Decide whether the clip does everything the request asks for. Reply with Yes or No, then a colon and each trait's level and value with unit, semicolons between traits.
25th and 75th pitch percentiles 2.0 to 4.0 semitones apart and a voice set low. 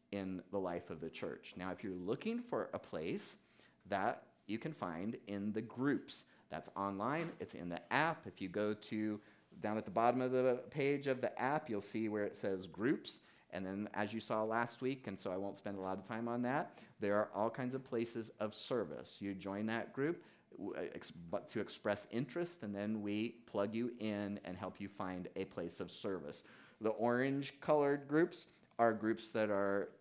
Yes: average, 3.4 semitones; low, 105 Hz